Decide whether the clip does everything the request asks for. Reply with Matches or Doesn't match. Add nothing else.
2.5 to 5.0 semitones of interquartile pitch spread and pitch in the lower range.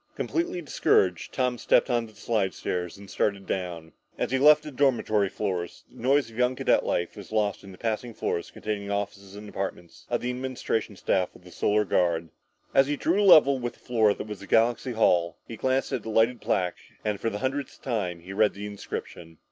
Matches